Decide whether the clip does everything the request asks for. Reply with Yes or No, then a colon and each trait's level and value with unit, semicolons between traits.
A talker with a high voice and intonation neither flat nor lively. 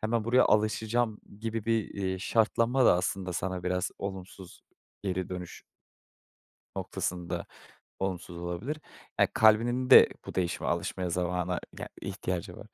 No: very low, 95 Hz; average, 3.7 semitones